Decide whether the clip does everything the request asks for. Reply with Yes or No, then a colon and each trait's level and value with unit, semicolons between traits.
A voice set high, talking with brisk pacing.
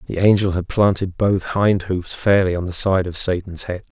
No: very low, 95 Hz; fast, 210 wpm